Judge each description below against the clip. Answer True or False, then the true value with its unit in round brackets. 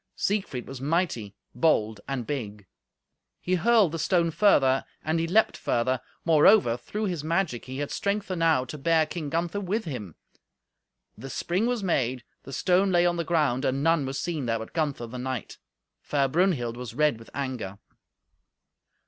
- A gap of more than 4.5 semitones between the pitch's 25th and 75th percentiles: True (5.5 semitones)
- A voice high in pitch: False (150 Hz)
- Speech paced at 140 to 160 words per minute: False (170 wpm)